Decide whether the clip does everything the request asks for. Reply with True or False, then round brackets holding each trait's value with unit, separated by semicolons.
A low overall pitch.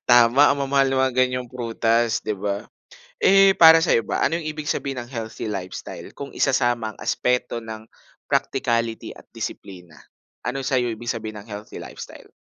True (120 Hz)